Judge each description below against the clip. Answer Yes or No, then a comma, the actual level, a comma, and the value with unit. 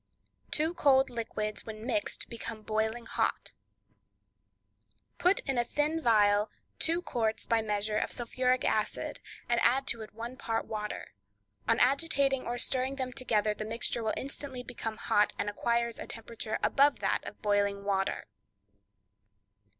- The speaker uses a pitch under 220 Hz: No, high, 235 Hz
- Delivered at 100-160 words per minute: Yes, average, 140 wpm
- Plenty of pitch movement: No, average, 3.5 semitones